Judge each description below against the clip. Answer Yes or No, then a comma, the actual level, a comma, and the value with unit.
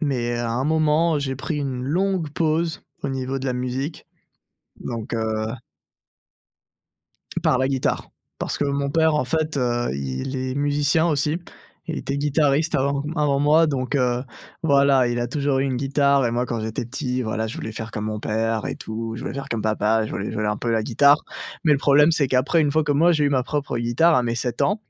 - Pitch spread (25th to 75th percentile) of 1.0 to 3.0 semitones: No, average, 3.7 semitones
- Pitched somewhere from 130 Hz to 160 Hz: Yes, low, 135 Hz